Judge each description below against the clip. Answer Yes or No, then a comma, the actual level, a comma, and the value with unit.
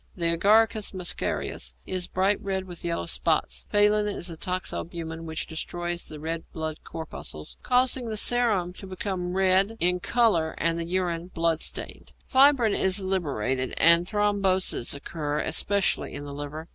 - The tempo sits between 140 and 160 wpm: Yes, average, 150 wpm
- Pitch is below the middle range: No, medium, 180 Hz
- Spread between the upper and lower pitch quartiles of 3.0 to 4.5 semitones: Yes, average, 3.6 semitones